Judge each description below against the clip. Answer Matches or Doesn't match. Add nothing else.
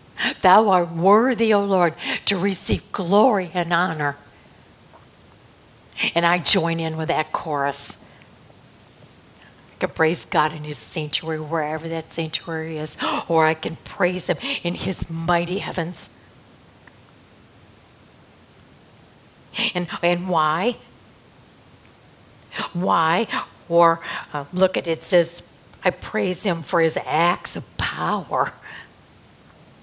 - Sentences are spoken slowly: Matches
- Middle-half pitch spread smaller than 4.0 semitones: Matches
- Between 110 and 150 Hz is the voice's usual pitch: Doesn't match